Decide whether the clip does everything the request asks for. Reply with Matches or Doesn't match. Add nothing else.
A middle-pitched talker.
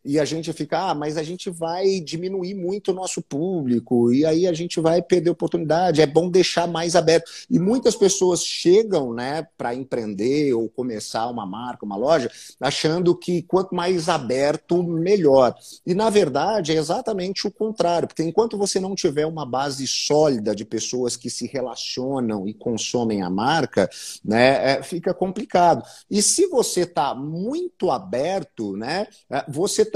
Matches